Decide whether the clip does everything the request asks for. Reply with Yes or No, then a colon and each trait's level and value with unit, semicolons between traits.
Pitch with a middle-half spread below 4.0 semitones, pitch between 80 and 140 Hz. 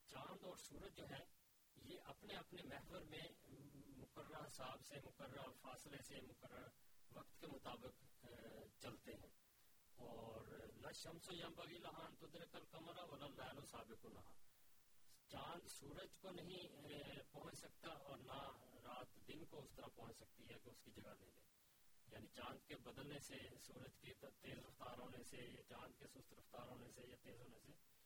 Yes: average, 3.6 semitones; low, 135 Hz